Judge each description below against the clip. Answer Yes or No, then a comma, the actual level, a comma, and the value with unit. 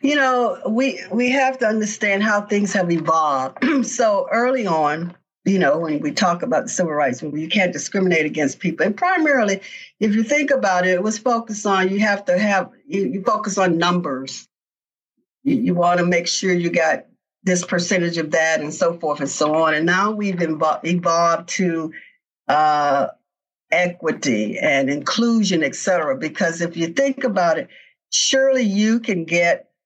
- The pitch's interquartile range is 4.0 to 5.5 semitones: Yes, average, 5.1 semitones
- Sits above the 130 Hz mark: Yes, medium, 185 Hz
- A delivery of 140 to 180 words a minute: Yes, average, 175 wpm